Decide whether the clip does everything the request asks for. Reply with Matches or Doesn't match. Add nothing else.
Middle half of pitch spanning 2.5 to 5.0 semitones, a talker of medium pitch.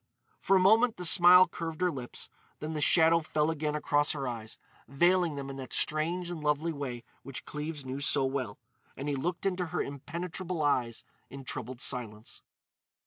Matches